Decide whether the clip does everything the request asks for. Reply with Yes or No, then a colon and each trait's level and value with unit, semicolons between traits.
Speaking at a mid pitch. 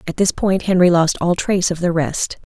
Yes: medium, 175 Hz